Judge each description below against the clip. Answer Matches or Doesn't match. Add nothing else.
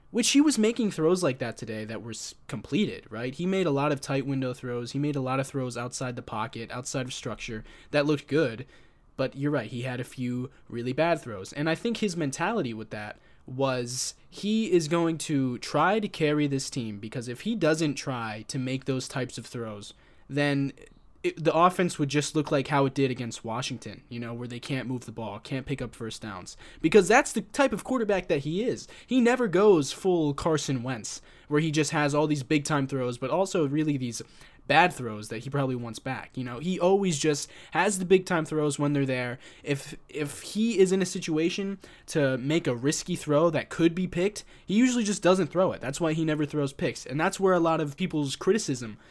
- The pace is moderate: Doesn't match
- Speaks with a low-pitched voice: Doesn't match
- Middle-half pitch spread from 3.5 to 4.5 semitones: Doesn't match